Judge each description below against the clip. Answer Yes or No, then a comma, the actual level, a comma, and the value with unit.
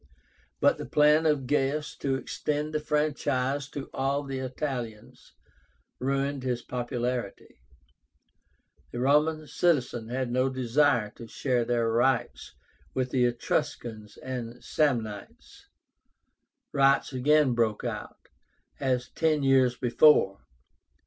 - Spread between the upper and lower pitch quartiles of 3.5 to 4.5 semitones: No, average, 3.1 semitones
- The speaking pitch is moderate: No, low, 130 Hz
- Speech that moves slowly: Yes, slow, 110 wpm